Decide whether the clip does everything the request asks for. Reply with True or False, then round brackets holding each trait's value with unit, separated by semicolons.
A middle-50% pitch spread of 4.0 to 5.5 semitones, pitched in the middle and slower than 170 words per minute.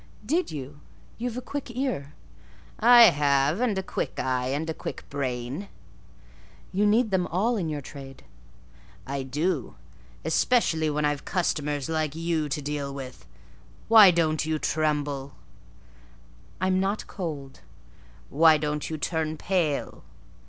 True (4.9 semitones; 155 Hz; 135 wpm)